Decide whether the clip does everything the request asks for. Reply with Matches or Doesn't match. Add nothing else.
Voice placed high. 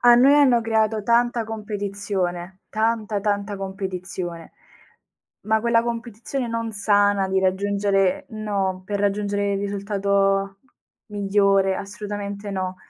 Matches